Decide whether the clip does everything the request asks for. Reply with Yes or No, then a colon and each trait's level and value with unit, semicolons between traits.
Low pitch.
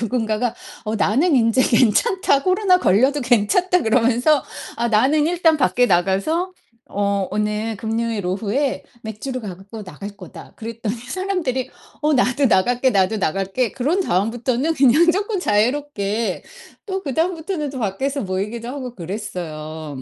No: high, 235 Hz